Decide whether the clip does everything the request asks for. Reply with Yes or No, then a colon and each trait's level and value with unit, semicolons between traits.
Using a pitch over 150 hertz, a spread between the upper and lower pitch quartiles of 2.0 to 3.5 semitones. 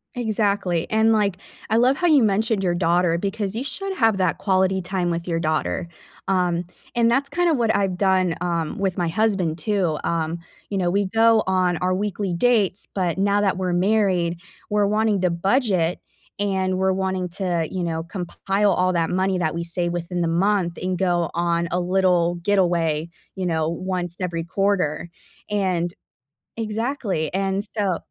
Yes: medium, 185 Hz; average, 2.9 semitones